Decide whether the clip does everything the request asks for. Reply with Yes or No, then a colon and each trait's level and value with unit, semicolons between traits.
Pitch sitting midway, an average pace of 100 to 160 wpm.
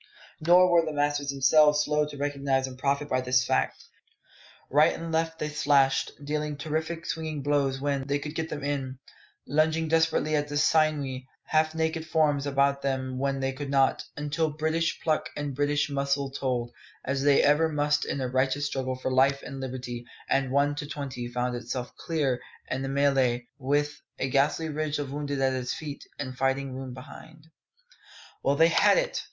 No: medium, 145 Hz; average, 180 wpm